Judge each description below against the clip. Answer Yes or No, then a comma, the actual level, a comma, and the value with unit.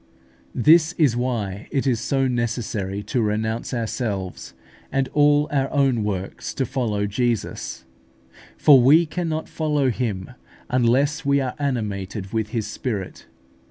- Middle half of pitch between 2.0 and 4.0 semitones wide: No, average, 4.8 semitones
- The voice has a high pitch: No, low, 125 Hz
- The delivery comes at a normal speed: No, slow, 130 wpm